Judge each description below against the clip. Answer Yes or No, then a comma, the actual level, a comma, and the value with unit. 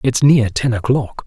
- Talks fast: No, average, 190 wpm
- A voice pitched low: Yes, low, 125 Hz